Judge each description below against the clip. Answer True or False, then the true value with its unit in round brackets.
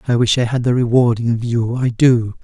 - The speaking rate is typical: False (220 wpm)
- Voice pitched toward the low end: True (120 Hz)